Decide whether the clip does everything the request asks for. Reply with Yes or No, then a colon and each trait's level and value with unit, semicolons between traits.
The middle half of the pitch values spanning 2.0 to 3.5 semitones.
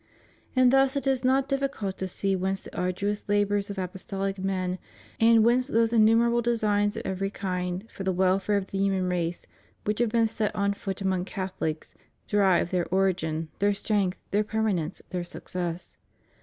Yes: average, 3.0 semitones